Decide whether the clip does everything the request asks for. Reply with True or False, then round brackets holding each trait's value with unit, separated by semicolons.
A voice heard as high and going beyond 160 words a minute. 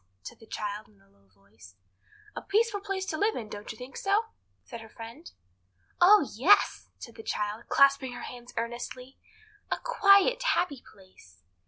True (245 Hz; 170 wpm)